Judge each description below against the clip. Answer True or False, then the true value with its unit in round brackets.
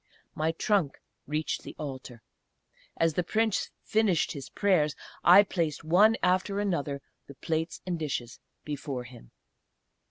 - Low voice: False (160 Hz)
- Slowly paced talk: True (130 wpm)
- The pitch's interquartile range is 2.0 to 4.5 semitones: False (4.9 semitones)